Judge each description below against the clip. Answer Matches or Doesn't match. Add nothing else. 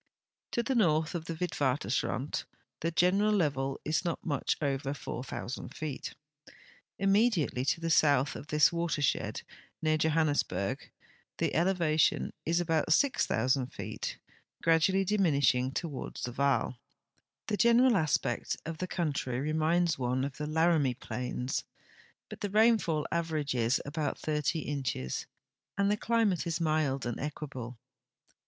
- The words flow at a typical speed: Doesn't match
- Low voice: Doesn't match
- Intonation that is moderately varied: Matches